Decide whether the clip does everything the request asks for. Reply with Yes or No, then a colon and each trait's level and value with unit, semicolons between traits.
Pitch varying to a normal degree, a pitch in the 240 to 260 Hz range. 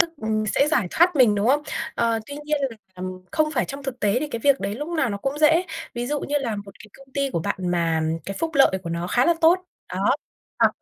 No: wide, 6.5 semitones; very high, 255 Hz